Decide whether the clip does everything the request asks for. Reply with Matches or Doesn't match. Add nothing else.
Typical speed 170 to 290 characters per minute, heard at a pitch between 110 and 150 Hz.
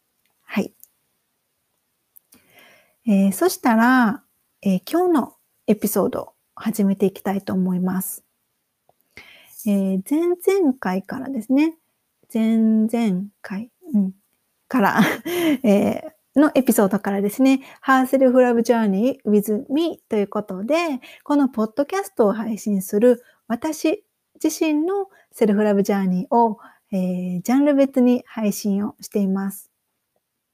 Doesn't match